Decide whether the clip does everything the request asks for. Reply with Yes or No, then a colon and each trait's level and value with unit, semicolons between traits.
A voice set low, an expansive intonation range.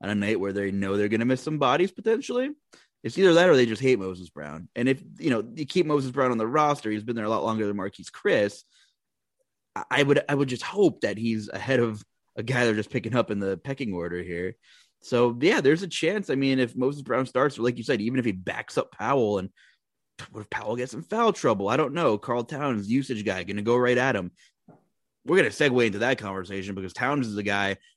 Yes: low, 120 Hz; wide, 5.8 semitones